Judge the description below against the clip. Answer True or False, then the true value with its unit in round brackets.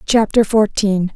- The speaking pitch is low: False (205 Hz)